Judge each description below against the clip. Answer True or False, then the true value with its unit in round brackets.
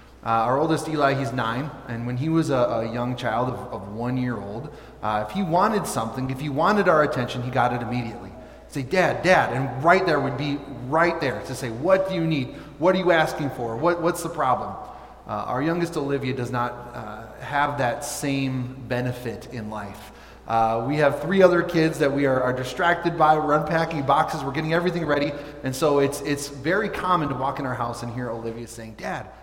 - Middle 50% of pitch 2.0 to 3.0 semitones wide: False (4.4 semitones)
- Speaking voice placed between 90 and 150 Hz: True (140 Hz)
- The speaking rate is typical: False (220 wpm)